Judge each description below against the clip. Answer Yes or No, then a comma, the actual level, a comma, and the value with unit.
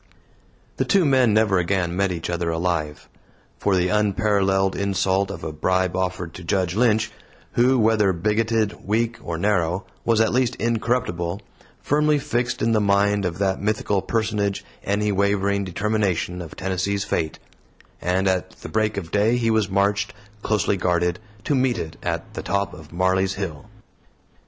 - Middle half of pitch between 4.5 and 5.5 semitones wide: No, average, 3.1 semitones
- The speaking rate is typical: Yes, average, 160 wpm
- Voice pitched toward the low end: Yes, low, 100 Hz